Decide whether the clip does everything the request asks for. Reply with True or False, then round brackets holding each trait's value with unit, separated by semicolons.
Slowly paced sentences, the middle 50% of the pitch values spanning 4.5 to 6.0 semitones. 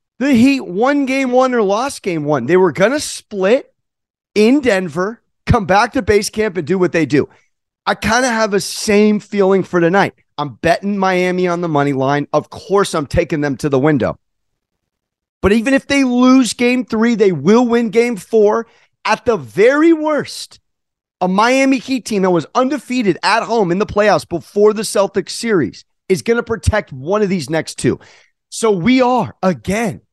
False (190 wpm; 5.1 semitones)